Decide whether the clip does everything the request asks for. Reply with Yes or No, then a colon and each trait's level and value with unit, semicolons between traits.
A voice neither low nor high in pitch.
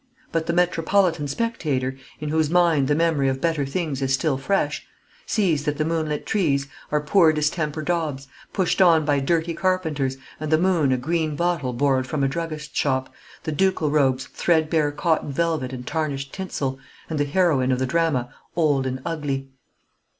Yes: medium, 150 Hz